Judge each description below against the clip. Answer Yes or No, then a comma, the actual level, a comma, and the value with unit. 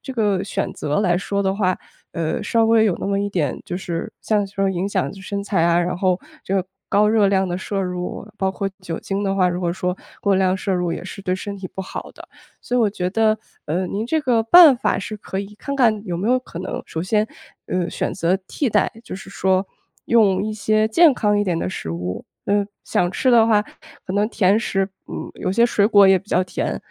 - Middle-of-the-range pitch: No, high, 195 Hz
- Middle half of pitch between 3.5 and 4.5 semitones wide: No, average, 2.7 semitones